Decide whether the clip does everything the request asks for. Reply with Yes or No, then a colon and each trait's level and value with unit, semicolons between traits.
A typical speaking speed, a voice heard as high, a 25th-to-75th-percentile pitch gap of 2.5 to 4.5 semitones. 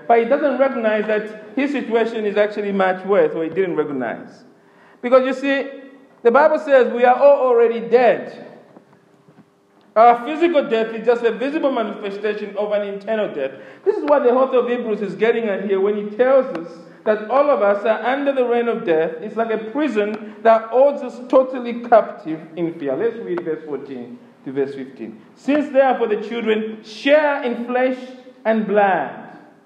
Yes: average, 180 wpm; high, 230 Hz; average, 4.1 semitones